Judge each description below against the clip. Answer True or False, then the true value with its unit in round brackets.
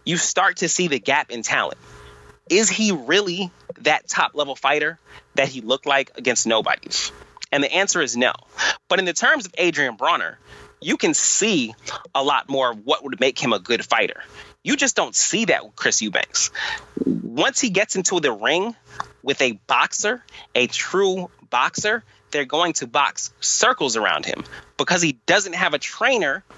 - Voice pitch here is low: False (180 Hz)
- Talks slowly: False (180 wpm)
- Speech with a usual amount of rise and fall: False (7.9 semitones)